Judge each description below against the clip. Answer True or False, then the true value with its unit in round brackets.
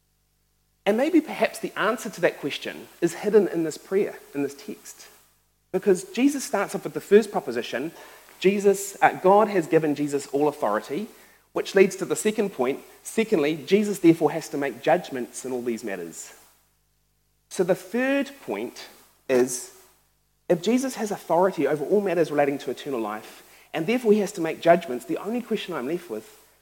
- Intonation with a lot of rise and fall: True (5.9 semitones)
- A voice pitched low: False (180 Hz)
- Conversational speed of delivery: True (175 wpm)